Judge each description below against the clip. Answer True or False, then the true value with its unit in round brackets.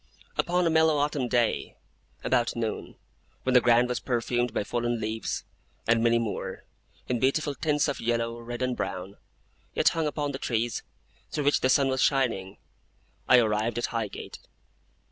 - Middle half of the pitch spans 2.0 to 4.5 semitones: True (2.9 semitones)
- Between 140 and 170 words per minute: True (165 wpm)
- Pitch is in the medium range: False (120 Hz)